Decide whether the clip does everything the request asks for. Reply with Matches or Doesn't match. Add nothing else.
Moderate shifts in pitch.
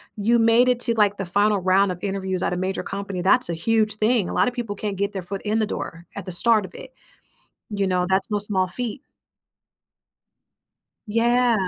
Matches